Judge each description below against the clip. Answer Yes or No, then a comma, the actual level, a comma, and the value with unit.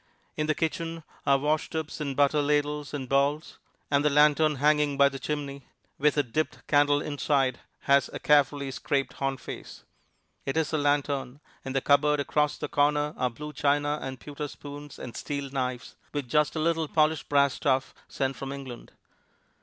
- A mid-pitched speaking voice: Yes, medium, 145 Hz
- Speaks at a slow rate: No, average, 175 wpm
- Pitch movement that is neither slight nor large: No, narrow, 1.4 semitones